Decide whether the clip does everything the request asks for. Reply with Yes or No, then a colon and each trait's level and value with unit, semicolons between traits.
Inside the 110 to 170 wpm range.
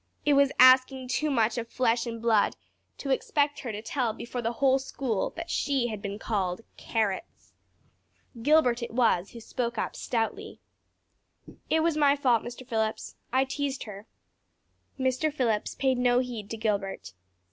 Yes: average, 160 wpm